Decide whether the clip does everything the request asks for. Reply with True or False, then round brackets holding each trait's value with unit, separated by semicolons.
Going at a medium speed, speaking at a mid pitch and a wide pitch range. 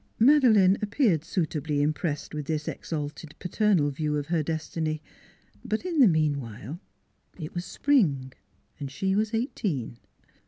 False (130 wpm; 160 Hz; 5.7 semitones)